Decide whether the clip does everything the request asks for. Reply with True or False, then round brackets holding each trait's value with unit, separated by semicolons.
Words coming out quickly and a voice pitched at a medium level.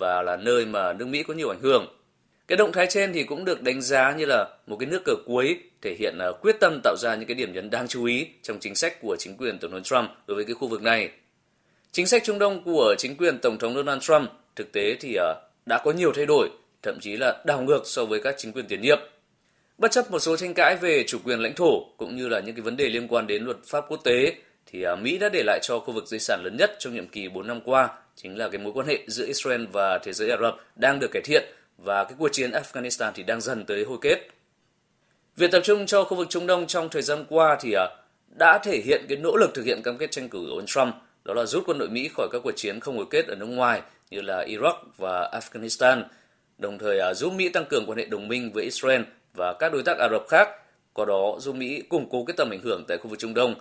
True (270 wpm; 175 Hz)